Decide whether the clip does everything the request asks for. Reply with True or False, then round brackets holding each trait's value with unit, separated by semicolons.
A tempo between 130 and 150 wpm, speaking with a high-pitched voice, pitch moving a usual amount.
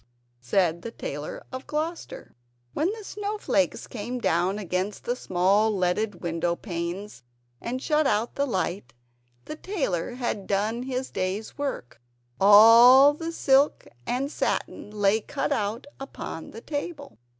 False (140 wpm; 220 Hz; 6.7 semitones)